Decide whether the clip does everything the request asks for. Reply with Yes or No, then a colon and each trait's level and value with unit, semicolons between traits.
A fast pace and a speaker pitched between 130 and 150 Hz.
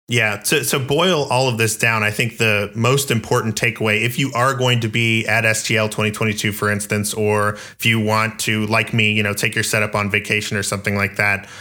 No: fast, 220 wpm; low, 110 Hz